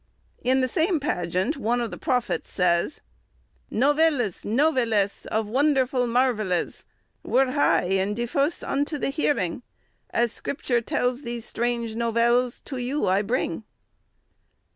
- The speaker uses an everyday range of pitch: Yes, average, 3.8 semitones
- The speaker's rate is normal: No, slow, 125 wpm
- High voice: Yes, high, 245 Hz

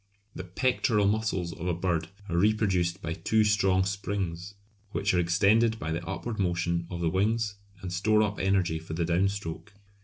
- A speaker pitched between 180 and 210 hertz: No, very low, 95 Hz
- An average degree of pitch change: Yes, average, 3.2 semitones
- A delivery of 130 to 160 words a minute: No, average, 180 wpm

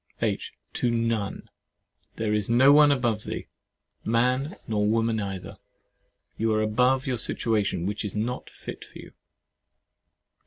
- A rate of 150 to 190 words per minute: No, average, 140 wpm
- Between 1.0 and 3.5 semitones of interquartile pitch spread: Yes, average, 2.9 semitones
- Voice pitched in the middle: No, low, 115 Hz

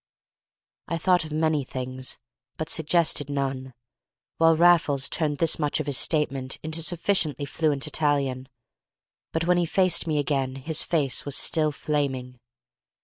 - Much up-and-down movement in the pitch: No, average, 3.0 semitones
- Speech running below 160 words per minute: Yes, average, 145 wpm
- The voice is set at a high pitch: No, medium, 150 Hz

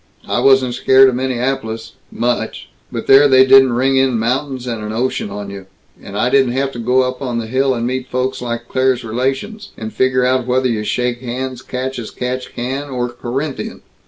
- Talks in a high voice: No, low, 125 Hz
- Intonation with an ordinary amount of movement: No, narrow, 1.8 semitones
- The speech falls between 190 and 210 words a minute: Yes, average, 200 wpm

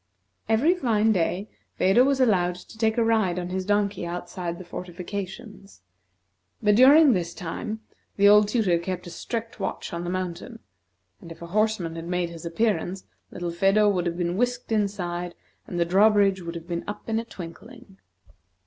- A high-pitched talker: Yes, high, 195 Hz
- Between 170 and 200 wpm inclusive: Yes, average, 180 wpm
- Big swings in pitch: No, average, 3.9 semitones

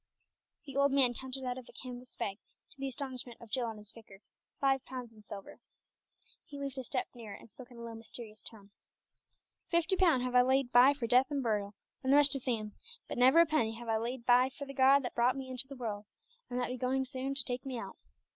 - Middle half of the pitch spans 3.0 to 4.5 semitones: No, narrow, 2.5 semitones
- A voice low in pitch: No, very high, 250 Hz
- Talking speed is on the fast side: Yes, fast, 240 wpm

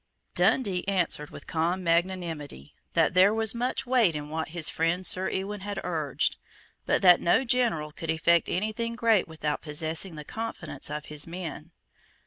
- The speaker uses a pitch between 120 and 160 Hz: No, medium, 175 Hz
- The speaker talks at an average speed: Yes, average, 165 wpm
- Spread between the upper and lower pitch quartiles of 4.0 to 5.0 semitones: Yes, average, 4.5 semitones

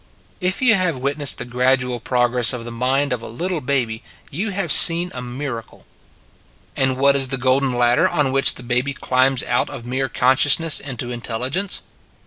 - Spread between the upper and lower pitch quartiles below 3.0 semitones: Yes, narrow, 2.6 semitones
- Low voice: Yes, low, 130 Hz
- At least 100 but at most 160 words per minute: No, average, 180 wpm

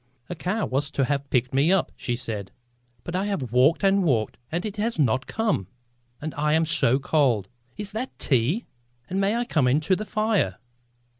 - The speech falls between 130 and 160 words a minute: No, average, 195 wpm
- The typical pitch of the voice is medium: Yes, medium, 155 Hz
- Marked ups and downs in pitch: Yes, wide, 7.6 semitones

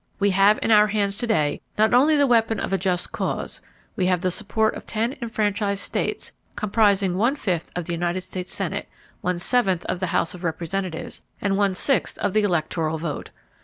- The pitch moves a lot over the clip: No, average, 3.3 semitones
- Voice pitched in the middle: No, high, 195 Hz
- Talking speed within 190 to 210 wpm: Yes, average, 200 wpm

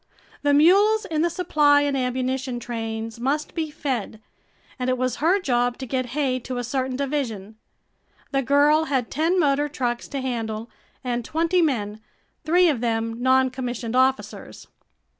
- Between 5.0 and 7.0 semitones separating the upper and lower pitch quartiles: No, average, 3.5 semitones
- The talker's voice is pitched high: Yes, very high, 260 Hz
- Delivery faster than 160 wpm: No, average, 155 wpm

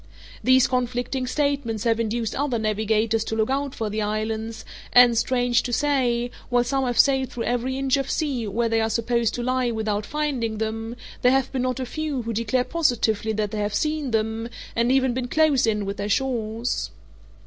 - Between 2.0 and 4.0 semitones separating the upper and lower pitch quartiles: Yes, average, 2.8 semitones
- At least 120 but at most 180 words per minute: No, average, 195 wpm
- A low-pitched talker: No, high, 240 Hz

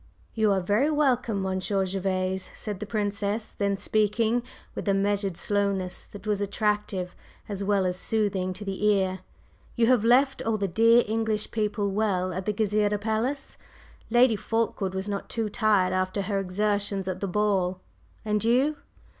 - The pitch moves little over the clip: Yes, narrow, 2.3 semitones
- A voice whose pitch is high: Yes, high, 205 Hz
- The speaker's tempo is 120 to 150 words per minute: No, average, 165 wpm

